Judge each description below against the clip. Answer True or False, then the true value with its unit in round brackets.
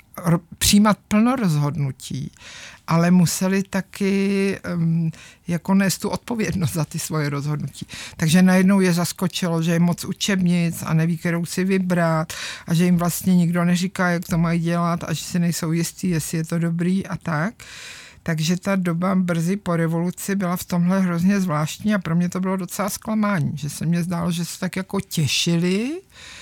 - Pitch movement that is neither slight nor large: False (2.2 semitones)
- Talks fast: True (175 wpm)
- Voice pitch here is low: False (175 Hz)